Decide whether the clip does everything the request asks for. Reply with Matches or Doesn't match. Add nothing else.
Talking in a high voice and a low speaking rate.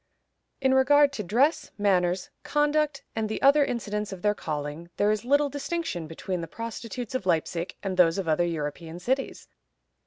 Doesn't match